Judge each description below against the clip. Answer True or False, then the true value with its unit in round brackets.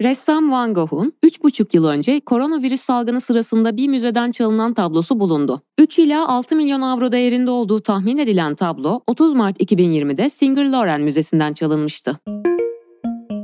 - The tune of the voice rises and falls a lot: True (7.5 semitones)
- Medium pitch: False (235 Hz)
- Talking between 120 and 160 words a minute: True (140 wpm)